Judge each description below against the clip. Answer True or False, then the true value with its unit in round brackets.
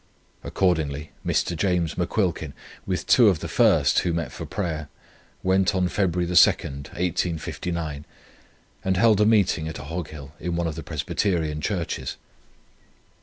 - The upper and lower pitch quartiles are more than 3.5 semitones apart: False (3.1 semitones)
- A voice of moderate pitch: False (85 Hz)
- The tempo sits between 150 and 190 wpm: False (135 wpm)